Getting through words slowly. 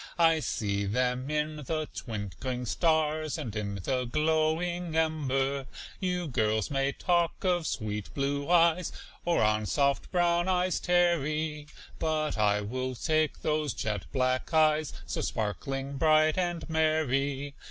Yes: slow, 130 wpm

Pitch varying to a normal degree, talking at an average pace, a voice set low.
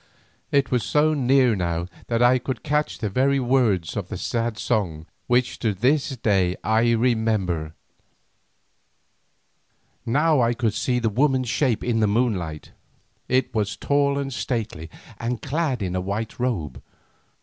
Yes: average, 4.3 semitones; average, 150 wpm; low, 115 Hz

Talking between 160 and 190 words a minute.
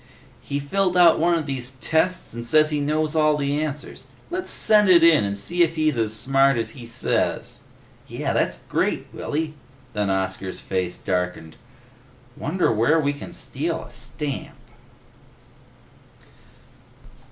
No: average, 145 wpm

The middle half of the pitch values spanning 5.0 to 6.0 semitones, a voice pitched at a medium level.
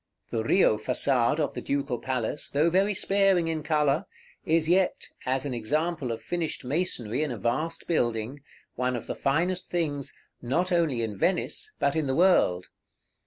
Yes: wide, 5.5 semitones; medium, 145 Hz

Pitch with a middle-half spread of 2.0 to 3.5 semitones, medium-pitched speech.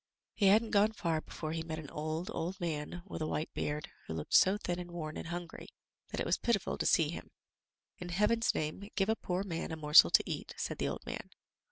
No: average, 3.9 semitones; medium, 170 Hz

